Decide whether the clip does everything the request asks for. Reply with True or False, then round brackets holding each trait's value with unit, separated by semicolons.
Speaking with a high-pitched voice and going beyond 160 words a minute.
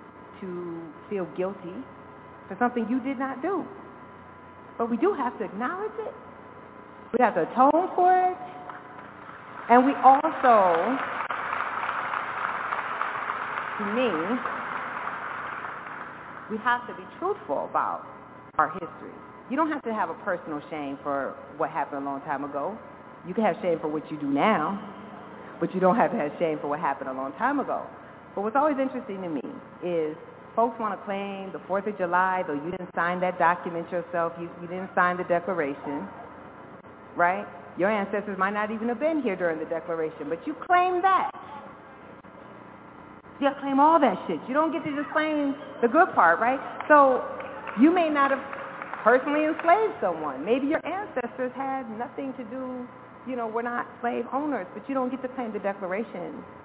True (230 Hz; 170 wpm)